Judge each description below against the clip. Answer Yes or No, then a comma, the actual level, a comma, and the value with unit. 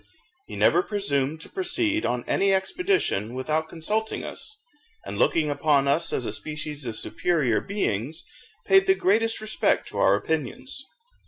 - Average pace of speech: Yes, average, 150 wpm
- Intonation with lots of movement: Yes, wide, 7.9 semitones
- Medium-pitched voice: Yes, medium, 160 Hz